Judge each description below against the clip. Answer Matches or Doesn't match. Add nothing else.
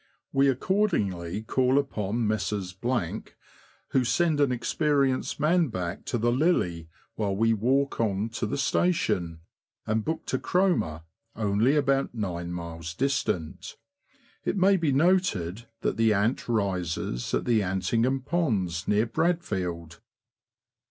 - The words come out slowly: Matches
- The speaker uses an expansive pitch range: Matches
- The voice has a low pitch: Matches